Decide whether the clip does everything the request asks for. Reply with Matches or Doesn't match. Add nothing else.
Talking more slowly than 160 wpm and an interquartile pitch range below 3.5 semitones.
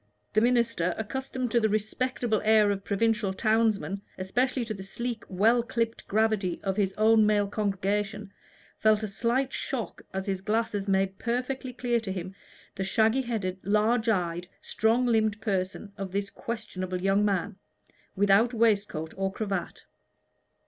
Matches